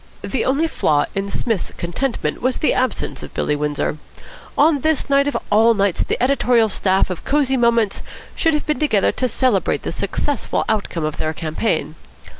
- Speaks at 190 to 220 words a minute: No, average, 175 wpm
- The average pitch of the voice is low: No, high, 230 Hz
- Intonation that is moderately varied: No, wide, 6.3 semitones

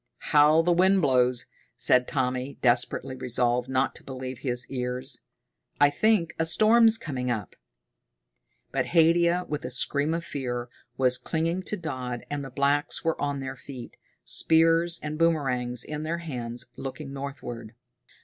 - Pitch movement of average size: Yes, average, 4.5 semitones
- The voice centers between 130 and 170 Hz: Yes, medium, 140 Hz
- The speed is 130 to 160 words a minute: Yes, average, 150 wpm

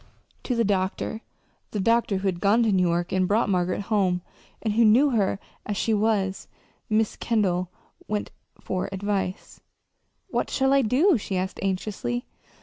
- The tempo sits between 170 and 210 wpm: No, average, 160 wpm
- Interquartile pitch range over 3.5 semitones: No, average, 3.1 semitones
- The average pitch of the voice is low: No, high, 205 Hz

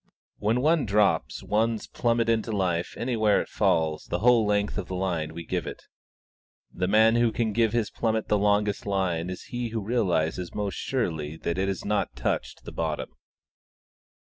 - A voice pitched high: No, low, 105 Hz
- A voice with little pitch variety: No, average, 3.9 semitones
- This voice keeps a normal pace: Yes, average, 175 wpm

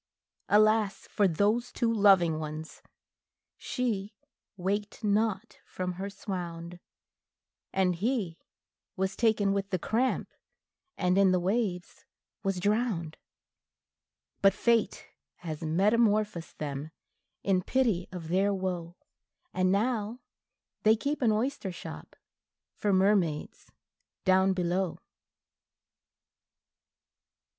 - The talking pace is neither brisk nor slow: No, slow, 100 wpm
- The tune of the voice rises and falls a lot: No, average, 3.1 semitones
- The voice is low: No, high, 195 Hz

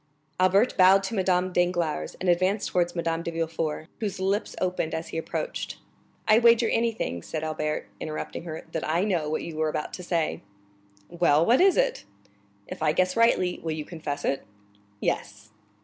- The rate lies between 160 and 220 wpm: Yes, average, 175 wpm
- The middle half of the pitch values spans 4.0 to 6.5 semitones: No, average, 3.5 semitones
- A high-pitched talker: No, medium, 175 Hz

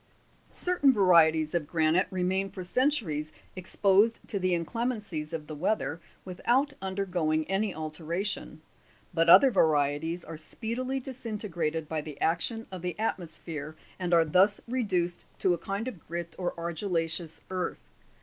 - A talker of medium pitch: Yes, medium, 180 Hz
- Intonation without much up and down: No, average, 4.3 semitones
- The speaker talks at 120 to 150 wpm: Yes, average, 140 wpm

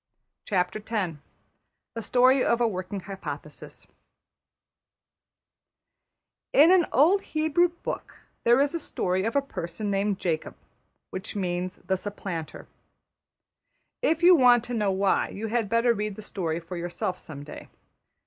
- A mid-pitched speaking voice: No, high, 210 Hz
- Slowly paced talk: Yes, slow, 130 wpm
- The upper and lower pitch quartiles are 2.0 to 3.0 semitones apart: No, average, 5.3 semitones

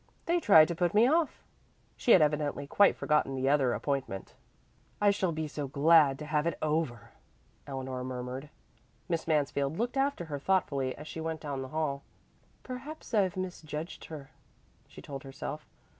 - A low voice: No, medium, 150 Hz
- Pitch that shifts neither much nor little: Yes, average, 4.1 semitones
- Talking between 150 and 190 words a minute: Yes, average, 165 wpm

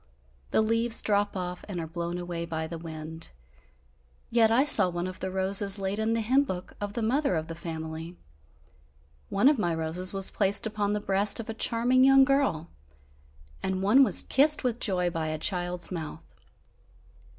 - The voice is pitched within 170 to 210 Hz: Yes, high, 190 Hz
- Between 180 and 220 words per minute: Yes, average, 185 wpm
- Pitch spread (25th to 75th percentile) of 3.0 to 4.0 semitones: No, average, 4.8 semitones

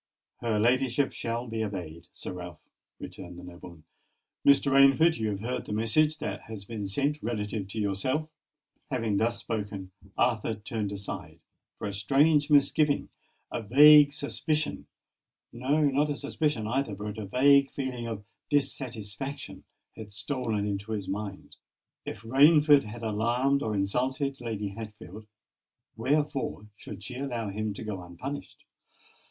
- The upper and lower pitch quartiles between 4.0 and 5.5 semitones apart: Yes, average, 5.1 semitones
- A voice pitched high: No, low, 115 Hz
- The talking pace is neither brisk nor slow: No, slow, 130 wpm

